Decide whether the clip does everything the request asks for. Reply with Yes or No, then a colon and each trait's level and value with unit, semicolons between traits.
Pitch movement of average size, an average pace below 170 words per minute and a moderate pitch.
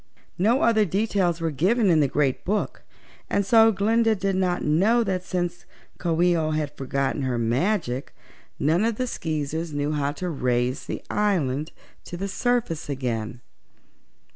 No: wide, 5.9 semitones; average, 160 wpm; medium, 170 Hz